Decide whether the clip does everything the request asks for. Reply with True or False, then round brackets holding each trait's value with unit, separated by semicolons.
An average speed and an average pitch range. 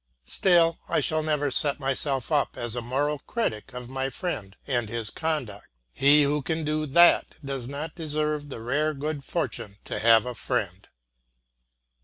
True (165 wpm; 3.9 semitones)